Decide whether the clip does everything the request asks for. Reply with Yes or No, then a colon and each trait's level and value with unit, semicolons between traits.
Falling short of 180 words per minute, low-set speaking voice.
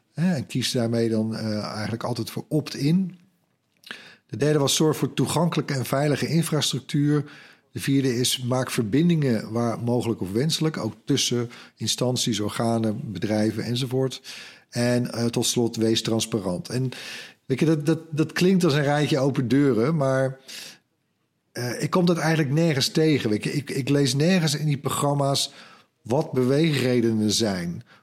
Yes: average, 150 wpm; low, 130 Hz